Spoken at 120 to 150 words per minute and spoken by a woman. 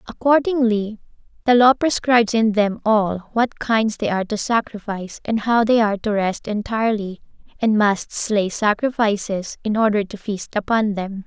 No: average, 160 wpm; female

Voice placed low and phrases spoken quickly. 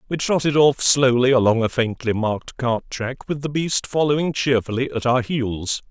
No: low, 125 Hz; average, 185 wpm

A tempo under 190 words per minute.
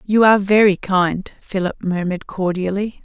Yes: average, 140 wpm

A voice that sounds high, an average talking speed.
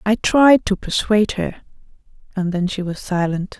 Yes: high, 200 Hz; average, 165 wpm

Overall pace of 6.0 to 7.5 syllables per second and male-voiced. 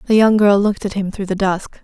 No: 6.1 syllables/s; female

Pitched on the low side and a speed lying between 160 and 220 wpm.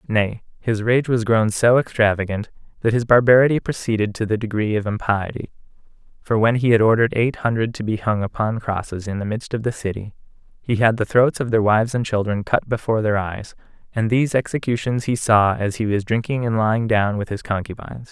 Yes: low, 110 Hz; fast, 205 wpm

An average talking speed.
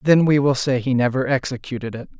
No: fast, 220 wpm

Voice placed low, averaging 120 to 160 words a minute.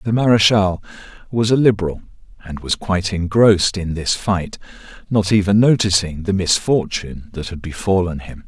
Yes: very low, 95 Hz; average, 150 wpm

